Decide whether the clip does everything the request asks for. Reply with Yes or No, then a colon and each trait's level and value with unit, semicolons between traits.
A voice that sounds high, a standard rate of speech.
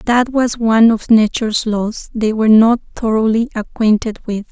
Yes: high, 225 Hz; average, 160 wpm